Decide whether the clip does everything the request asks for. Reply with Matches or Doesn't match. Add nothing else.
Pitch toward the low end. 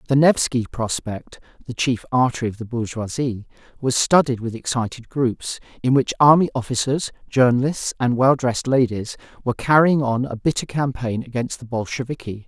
Matches